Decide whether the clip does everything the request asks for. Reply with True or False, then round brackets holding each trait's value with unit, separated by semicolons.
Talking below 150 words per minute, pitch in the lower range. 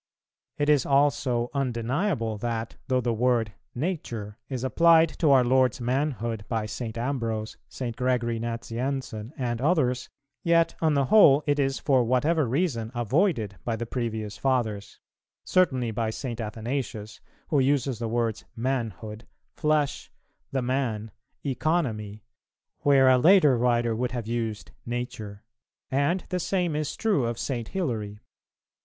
True (135 wpm; 125 Hz)